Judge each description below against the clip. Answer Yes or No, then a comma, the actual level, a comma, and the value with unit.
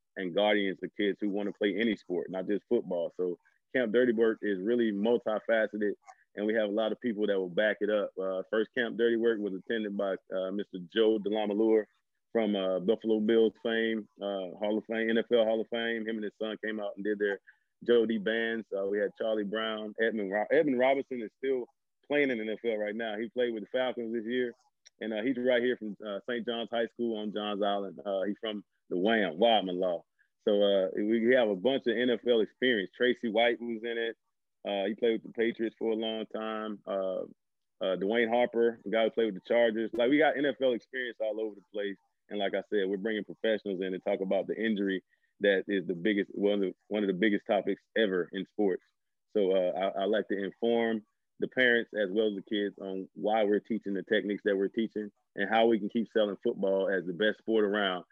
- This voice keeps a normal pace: No, fast, 225 wpm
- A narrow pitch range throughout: Yes, narrow, 2.3 semitones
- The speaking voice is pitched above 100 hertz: Yes, low, 110 Hz